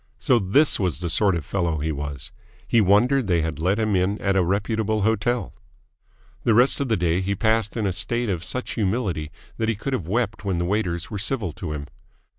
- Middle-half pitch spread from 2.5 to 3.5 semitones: No, average, 4.4 semitones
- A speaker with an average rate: No, fast, 220 wpm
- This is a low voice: Yes, low, 100 Hz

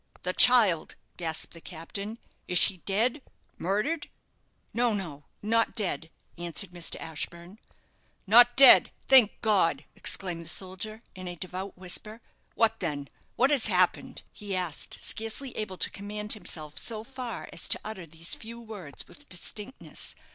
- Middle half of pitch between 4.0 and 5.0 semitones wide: Yes, average, 4.5 semitones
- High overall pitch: Yes, high, 200 Hz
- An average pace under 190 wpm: Yes, average, 145 wpm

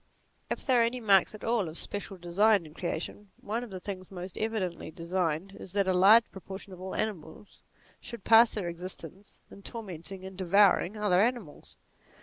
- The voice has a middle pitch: No, high, 195 Hz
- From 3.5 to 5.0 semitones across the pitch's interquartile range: No, average, 3.1 semitones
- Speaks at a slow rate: No, average, 180 wpm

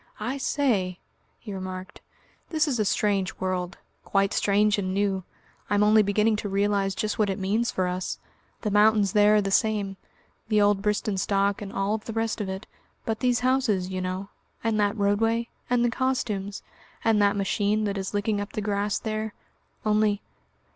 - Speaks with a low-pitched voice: No, high, 205 Hz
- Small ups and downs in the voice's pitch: Yes, narrow, 1.8 semitones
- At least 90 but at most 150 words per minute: No, average, 175 wpm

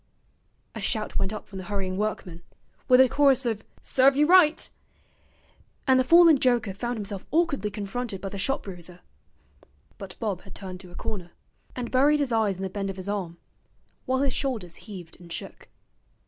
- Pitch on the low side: No, high, 210 Hz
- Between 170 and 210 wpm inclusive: Yes, average, 185 wpm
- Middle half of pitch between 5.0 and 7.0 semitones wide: Yes, wide, 5.4 semitones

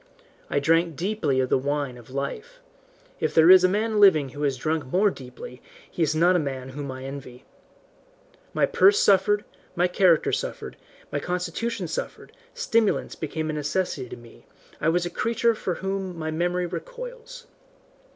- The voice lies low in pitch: No, medium, 170 Hz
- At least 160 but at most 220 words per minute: Yes, average, 170 wpm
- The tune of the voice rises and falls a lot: Yes, wide, 5.7 semitones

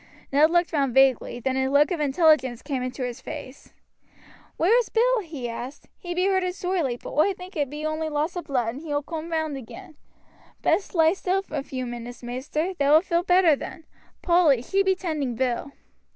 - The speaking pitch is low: No, very high, 305 Hz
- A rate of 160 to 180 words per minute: No, average, 200 wpm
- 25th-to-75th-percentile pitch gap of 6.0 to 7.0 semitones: No, average, 5.1 semitones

